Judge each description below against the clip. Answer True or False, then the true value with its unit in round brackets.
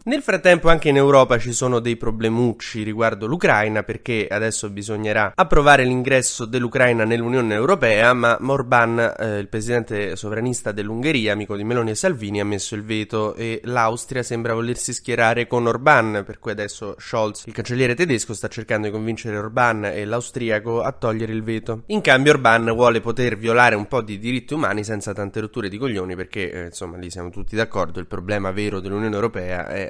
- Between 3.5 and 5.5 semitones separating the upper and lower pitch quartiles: False (2.5 semitones)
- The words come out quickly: True (180 wpm)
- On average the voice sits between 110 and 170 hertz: True (115 Hz)